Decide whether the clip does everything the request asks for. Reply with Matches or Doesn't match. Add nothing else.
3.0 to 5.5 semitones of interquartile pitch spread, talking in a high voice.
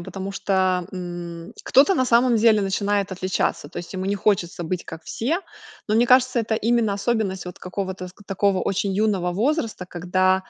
Matches